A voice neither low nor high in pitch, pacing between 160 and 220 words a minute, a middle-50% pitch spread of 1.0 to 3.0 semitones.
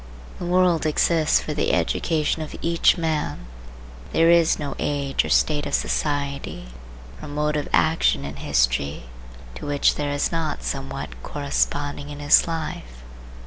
No: medium, 145 Hz; average, 145 wpm; narrow, 2.6 semitones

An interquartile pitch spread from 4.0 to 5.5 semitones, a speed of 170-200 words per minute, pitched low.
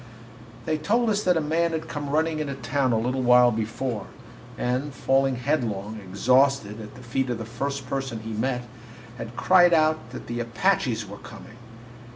Yes: average, 4.4 semitones; average, 180 wpm; low, 130 Hz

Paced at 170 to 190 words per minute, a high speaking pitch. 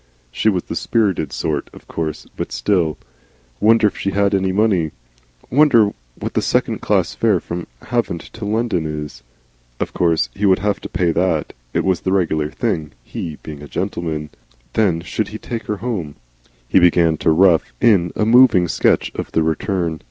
No: average, 180 wpm; very low, 90 Hz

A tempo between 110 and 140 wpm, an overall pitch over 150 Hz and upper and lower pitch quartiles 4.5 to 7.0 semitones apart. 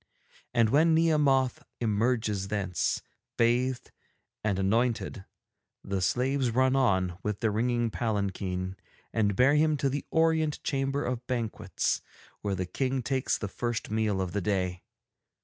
No: slow, 135 wpm; low, 115 Hz; average, 4.9 semitones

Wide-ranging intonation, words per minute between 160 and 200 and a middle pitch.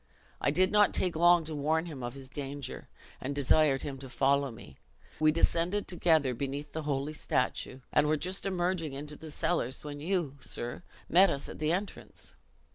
No: average, 3.7 semitones; average, 185 wpm; medium, 150 Hz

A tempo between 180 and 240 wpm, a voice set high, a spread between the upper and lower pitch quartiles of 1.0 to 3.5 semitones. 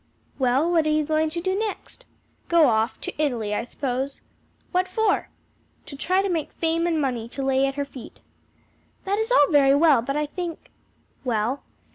No: average, 190 wpm; very high, 295 Hz; average, 4.4 semitones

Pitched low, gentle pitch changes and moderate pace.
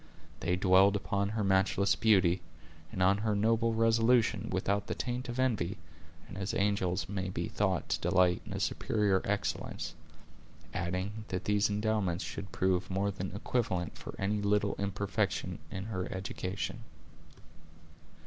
Yes: low, 100 Hz; narrow, 2.2 semitones; average, 145 wpm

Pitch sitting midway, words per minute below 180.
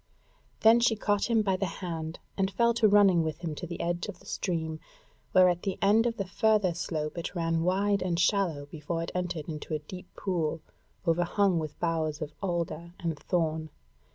No: medium, 175 Hz; average, 195 wpm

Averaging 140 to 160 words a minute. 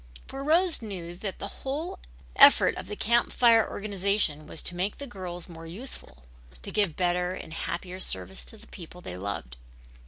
No: average, 180 wpm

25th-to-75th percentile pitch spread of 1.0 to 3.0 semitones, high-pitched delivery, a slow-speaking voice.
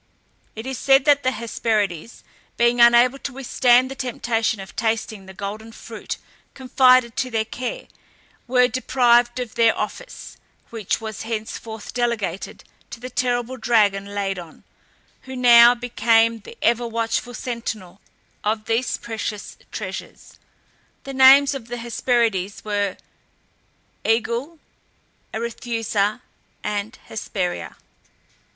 Yes: narrow, 2.5 semitones; high, 235 Hz; slow, 120 wpm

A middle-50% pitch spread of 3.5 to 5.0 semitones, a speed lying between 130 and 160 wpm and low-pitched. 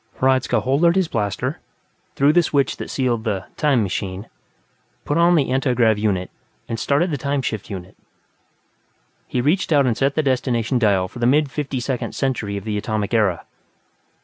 No: average, 4.7 semitones; average, 175 wpm; low, 125 Hz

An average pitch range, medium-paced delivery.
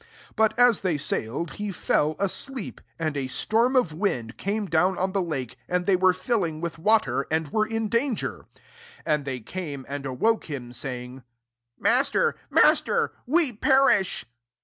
No: wide, 7.4 semitones; average, 165 wpm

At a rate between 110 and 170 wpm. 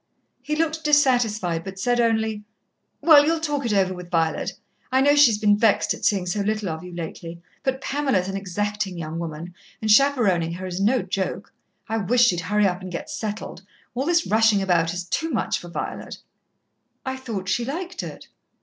No: average, 190 wpm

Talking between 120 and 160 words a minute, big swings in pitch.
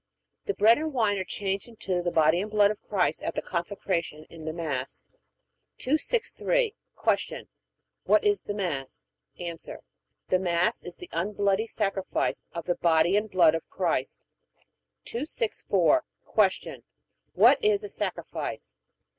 No: average, 140 wpm; average, 4.5 semitones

